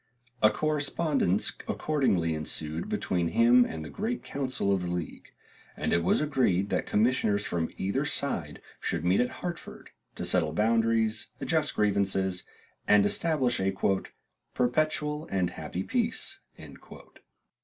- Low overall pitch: Yes, low, 105 Hz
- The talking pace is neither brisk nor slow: No, slow, 130 wpm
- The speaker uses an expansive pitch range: Yes, wide, 7.7 semitones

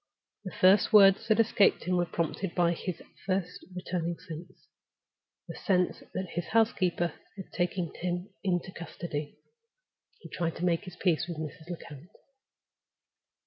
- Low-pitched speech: No, medium, 180 Hz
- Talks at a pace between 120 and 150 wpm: Yes, average, 140 wpm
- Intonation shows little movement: Yes, narrow, 1.8 semitones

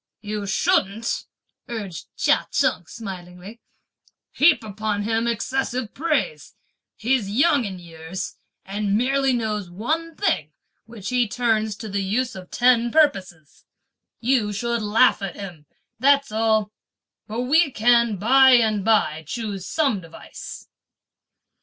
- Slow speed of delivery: Yes, slow, 125 wpm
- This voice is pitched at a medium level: No, high, 220 Hz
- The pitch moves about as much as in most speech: Yes, average, 4.2 semitones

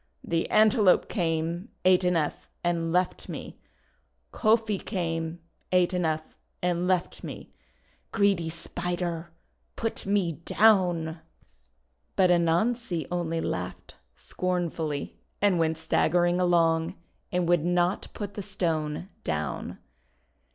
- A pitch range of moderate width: No, narrow, 2.2 semitones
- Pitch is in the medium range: Yes, medium, 175 Hz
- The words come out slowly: Yes, slow, 105 wpm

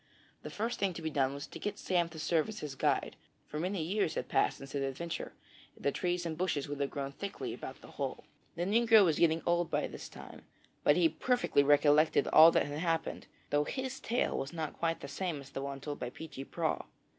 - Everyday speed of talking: No, fast, 230 wpm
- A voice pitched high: No, medium, 160 Hz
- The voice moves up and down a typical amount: Yes, average, 3.8 semitones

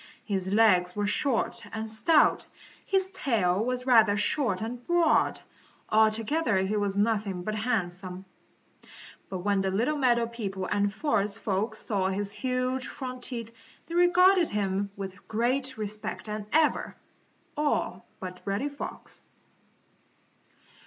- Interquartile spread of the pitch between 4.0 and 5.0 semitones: Yes, average, 4.3 semitones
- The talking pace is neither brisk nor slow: No, slow, 130 wpm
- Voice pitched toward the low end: No, high, 220 Hz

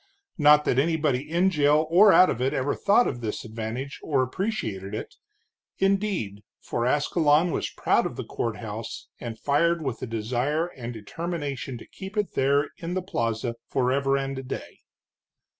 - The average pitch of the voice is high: No, medium, 140 Hz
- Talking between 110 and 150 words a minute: No, average, 165 wpm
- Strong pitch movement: Yes, wide, 5.9 semitones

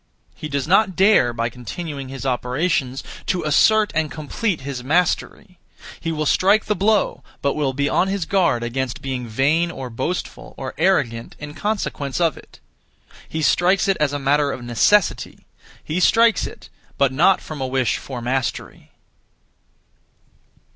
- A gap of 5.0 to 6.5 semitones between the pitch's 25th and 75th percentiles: Yes, wide, 5.5 semitones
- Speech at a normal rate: Yes, average, 155 wpm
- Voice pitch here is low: No, medium, 150 Hz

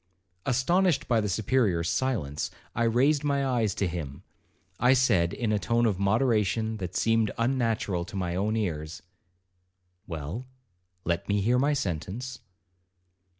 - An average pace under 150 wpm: Yes, average, 140 wpm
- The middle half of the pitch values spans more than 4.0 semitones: Yes, wide, 5.6 semitones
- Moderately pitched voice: No, low, 110 Hz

